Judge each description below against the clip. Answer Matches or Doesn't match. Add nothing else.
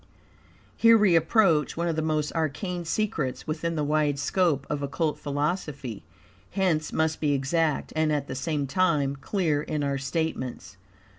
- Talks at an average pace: Matches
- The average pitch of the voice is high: Doesn't match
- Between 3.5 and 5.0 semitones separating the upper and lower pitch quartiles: Doesn't match